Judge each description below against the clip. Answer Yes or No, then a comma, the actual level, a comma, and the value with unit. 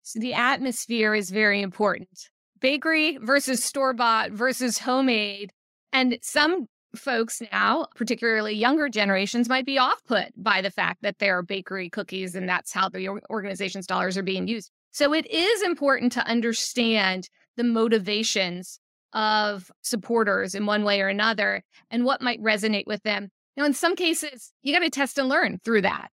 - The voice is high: Yes, high, 225 Hz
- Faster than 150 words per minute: Yes, average, 165 wpm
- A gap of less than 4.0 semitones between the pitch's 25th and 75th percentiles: No, average, 4.3 semitones